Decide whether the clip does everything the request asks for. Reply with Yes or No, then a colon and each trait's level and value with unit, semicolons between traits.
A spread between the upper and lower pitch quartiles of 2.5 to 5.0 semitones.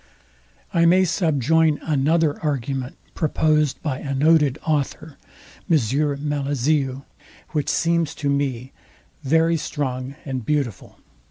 Yes: average, 2.8 semitones